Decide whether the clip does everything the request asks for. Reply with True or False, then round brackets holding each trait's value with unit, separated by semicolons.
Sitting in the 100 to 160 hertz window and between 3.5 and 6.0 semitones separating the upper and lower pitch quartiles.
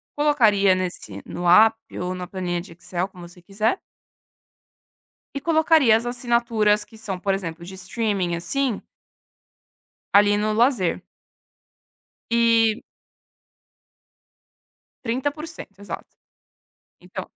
False (210 Hz; 4.4 semitones)